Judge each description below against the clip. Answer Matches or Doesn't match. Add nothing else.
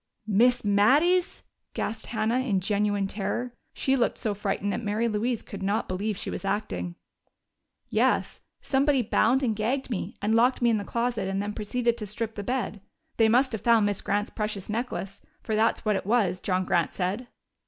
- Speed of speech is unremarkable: Matches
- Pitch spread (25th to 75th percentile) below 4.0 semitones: Matches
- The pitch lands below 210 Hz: Doesn't match